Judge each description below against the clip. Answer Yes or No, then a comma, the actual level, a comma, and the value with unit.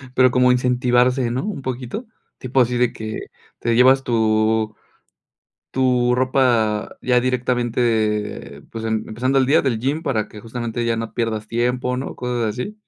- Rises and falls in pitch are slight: Yes, narrow, 2.2 semitones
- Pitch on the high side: No, low, 125 Hz